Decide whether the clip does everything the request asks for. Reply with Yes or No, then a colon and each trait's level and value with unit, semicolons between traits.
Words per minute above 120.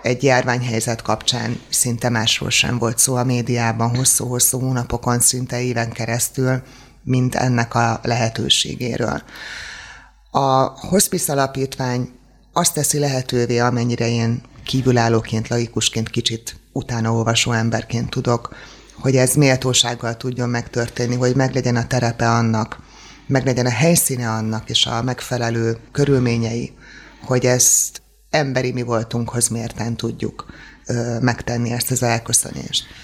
No: average, 115 wpm